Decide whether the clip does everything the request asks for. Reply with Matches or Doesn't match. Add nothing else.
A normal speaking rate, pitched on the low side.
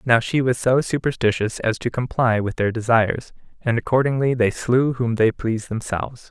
Matches